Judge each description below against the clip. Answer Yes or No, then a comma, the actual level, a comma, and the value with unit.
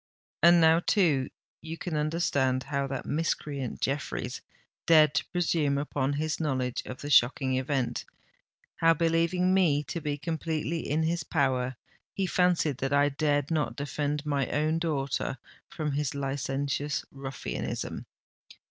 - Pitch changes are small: No, average, 3.0 semitones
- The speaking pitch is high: No, medium, 145 Hz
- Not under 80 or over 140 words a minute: Yes, slow, 135 wpm